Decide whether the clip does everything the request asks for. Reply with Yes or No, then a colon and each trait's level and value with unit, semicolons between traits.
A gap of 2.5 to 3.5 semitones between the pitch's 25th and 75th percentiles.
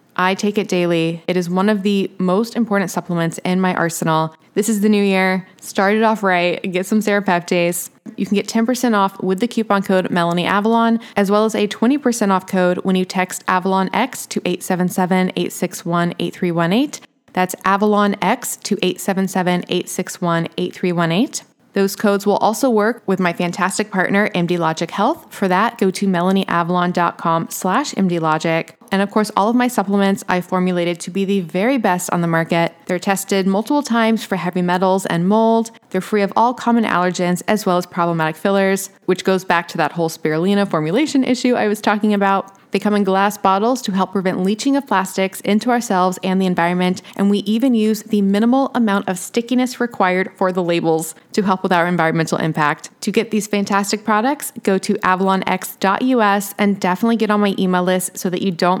Yes: average, 2.8 semitones